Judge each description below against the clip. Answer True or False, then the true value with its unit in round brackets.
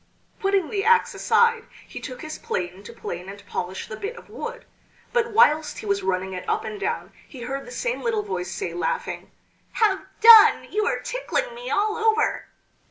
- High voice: True (395 Hz)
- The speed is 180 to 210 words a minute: True (190 wpm)